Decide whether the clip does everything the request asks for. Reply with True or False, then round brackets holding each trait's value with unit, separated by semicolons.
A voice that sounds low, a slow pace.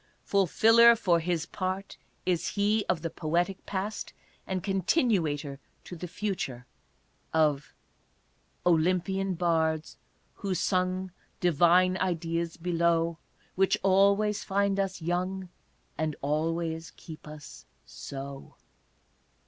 False (175 Hz; 105 wpm)